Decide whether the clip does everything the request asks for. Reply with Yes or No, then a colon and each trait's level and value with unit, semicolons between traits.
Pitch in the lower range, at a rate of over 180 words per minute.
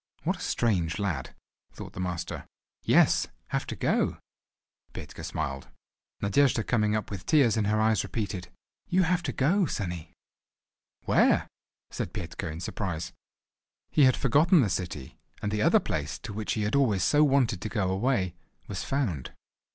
No: low, 105 Hz; average, 160 wpm